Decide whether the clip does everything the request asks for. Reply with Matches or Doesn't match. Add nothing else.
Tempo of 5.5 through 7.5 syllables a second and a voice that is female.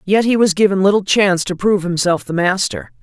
Matches